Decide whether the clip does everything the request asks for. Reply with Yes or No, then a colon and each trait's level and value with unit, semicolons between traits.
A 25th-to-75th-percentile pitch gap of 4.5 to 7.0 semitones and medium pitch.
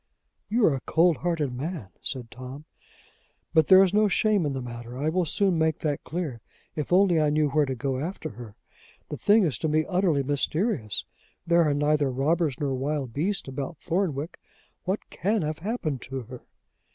Yes: average, 4.8 semitones; medium, 150 Hz